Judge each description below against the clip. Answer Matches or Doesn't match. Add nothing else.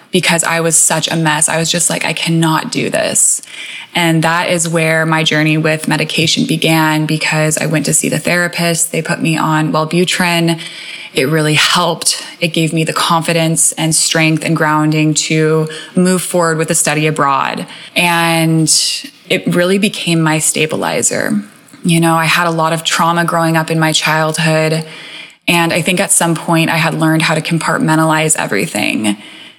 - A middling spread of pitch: Doesn't match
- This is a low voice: Doesn't match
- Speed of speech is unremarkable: Matches